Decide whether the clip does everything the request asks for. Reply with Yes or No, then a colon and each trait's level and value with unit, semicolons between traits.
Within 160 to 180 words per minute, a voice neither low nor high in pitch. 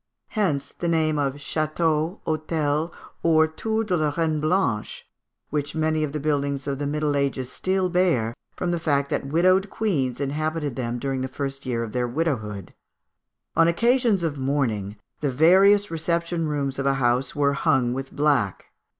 Yes: average, 165 wpm; medium, 150 Hz